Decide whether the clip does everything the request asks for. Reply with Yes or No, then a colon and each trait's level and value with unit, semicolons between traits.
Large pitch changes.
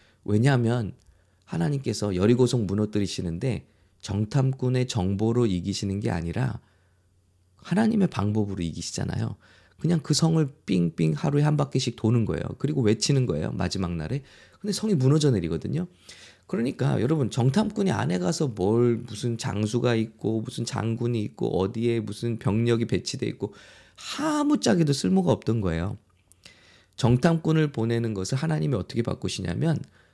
Yes: wide, 6.4 semitones